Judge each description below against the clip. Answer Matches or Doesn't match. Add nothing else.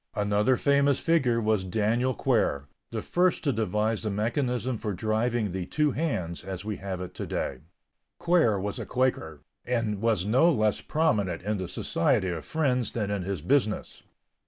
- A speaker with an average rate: Matches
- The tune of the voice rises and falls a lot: Doesn't match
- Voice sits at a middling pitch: Doesn't match